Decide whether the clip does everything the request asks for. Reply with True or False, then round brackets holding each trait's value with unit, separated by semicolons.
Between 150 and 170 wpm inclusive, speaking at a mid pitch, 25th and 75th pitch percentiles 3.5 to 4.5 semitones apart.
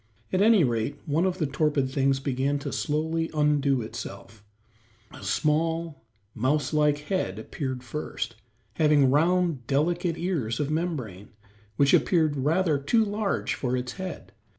False (140 wpm; 150 Hz; 4.0 semitones)